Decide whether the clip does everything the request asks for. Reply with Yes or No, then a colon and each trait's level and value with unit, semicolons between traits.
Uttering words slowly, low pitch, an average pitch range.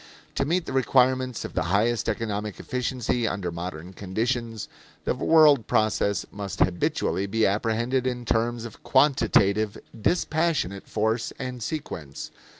Yes: slow, 130 wpm; low, 115 Hz; average, 4.1 semitones